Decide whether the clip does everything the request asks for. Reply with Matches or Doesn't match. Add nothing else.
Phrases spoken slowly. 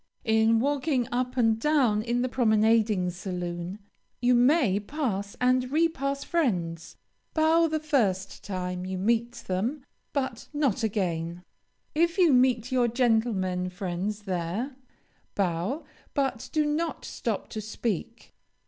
Matches